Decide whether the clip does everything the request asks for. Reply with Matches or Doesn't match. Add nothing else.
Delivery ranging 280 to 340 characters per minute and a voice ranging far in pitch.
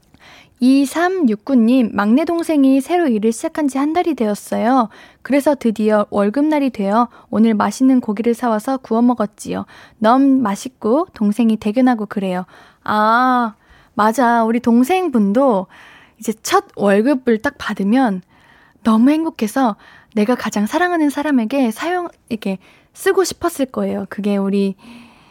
Doesn't match